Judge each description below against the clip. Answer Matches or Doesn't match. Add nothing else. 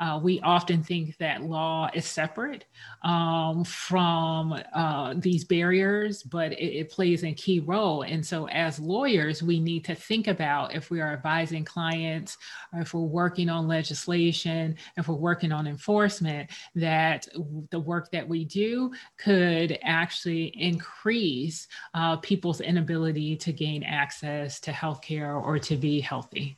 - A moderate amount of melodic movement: Doesn't match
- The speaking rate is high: Doesn't match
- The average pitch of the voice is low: Doesn't match